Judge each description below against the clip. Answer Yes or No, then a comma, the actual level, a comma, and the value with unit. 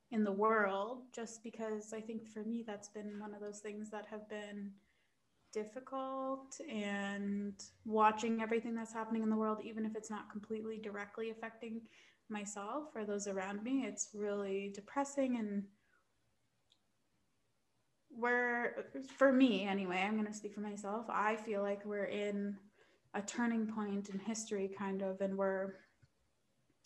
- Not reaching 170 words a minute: Yes, average, 150 wpm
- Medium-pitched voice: No, high, 215 Hz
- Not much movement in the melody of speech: Yes, narrow, 1.9 semitones